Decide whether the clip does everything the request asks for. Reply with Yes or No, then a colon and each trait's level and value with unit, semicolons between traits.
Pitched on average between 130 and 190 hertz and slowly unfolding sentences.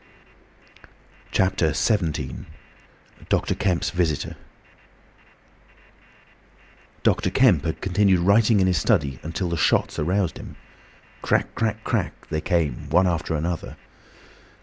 No: very low, 85 Hz; slow, 110 wpm